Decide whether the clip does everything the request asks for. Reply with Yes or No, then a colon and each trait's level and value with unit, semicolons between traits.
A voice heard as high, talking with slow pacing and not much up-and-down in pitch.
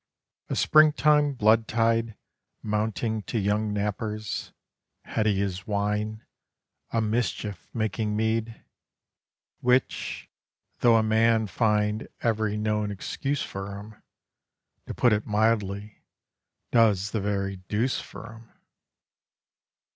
No: low, 110 Hz; slow, 110 wpm; narrow, 1.6 semitones